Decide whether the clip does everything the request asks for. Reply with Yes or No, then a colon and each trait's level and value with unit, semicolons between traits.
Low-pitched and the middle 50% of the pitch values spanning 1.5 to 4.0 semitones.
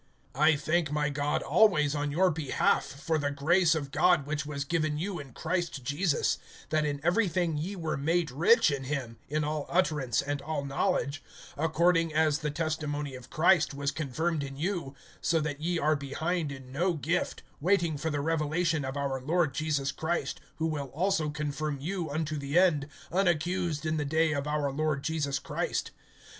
No: medium, 155 Hz; average, 2.7 semitones